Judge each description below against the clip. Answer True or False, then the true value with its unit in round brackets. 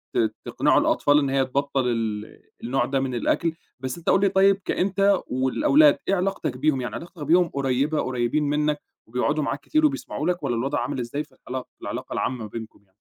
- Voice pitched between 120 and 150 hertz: True (140 Hz)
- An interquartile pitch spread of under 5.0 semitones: False (5.6 semitones)